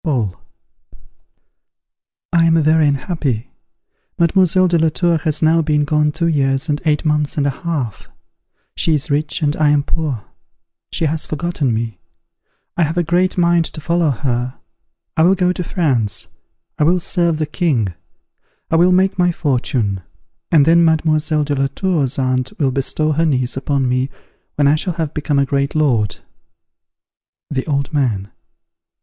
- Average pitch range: Yes, average, 3.4 semitones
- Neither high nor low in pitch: Yes, medium, 150 Hz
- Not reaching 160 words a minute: No, average, 165 wpm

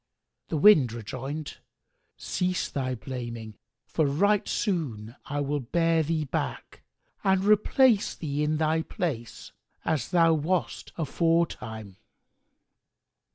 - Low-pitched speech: No, medium, 155 Hz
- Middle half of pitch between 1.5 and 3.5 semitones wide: No, average, 4.9 semitones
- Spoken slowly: Yes, slow, 110 wpm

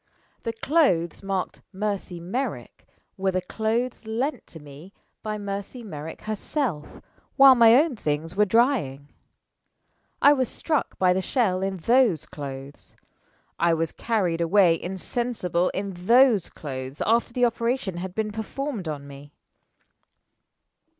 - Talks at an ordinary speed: No, slow, 130 wpm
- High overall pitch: Yes, high, 195 Hz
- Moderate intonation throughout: No, wide, 5.9 semitones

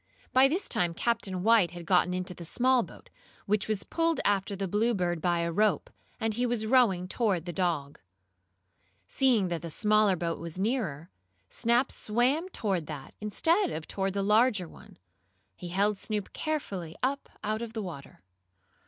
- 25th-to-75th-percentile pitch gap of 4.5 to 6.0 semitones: Yes, average, 5.1 semitones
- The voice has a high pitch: Yes, high, 205 Hz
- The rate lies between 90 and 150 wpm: No, average, 170 wpm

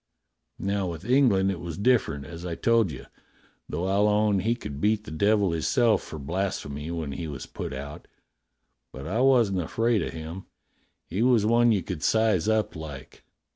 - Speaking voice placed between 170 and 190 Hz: No, very low, 95 Hz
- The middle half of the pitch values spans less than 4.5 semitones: No, wide, 5.4 semitones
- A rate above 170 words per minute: Yes, average, 180 wpm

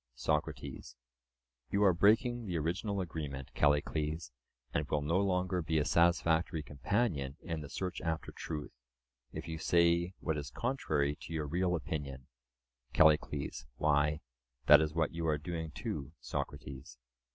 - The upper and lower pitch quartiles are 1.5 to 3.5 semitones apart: Yes, average, 3.1 semitones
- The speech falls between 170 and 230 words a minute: No, average, 140 wpm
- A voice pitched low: Yes, very low, 80 Hz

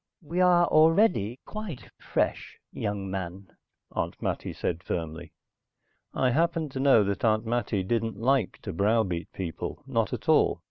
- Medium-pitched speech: No, low, 115 Hz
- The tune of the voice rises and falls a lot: Yes, wide, 7.5 semitones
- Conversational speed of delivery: Yes, average, 145 wpm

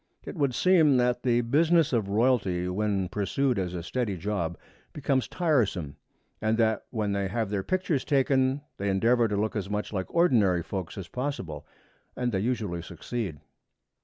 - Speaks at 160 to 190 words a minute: Yes, average, 165 wpm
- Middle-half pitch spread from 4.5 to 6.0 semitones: Yes, average, 5.2 semitones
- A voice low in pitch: Yes, low, 110 Hz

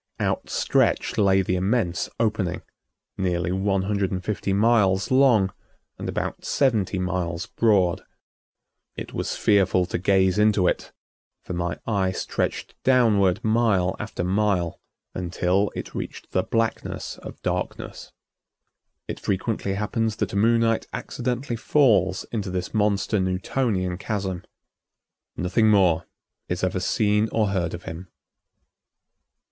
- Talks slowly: Yes, slow, 125 wpm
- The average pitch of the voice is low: Yes, very low, 95 Hz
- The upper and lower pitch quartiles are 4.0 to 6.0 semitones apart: No, average, 2.9 semitones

